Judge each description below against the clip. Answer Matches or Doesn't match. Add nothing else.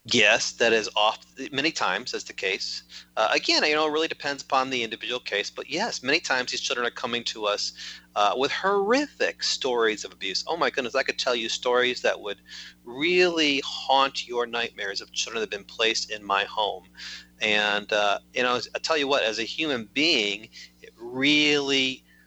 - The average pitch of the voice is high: Doesn't match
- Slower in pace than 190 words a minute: Doesn't match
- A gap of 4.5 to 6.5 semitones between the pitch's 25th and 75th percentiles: Matches